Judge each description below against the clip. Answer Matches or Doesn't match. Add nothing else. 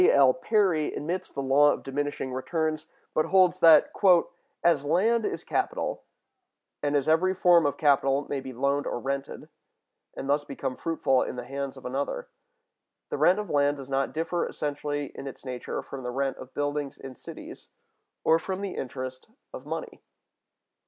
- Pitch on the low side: Doesn't match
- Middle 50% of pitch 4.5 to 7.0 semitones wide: Doesn't match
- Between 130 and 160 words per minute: Doesn't match